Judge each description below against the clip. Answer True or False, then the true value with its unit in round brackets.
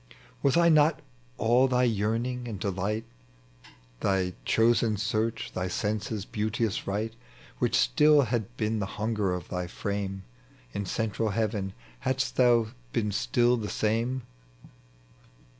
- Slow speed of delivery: True (125 wpm)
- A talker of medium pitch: False (110 Hz)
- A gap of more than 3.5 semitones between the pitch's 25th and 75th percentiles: False (2.9 semitones)